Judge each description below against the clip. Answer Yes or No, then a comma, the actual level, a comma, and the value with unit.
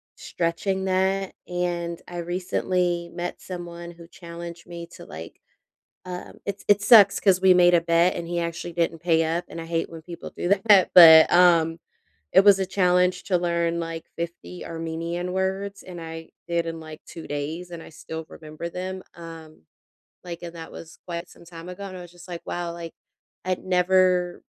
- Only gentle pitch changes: Yes, narrow, 1.4 semitones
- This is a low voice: No, medium, 175 Hz